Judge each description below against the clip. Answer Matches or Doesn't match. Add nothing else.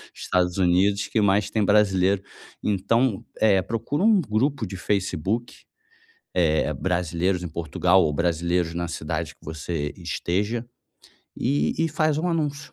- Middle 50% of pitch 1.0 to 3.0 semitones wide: Doesn't match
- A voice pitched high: Doesn't match